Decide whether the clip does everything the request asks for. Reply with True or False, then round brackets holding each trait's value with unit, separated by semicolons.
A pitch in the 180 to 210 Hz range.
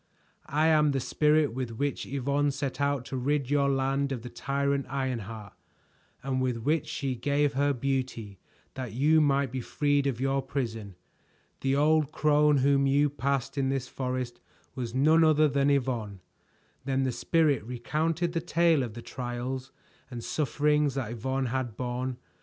False (135 Hz)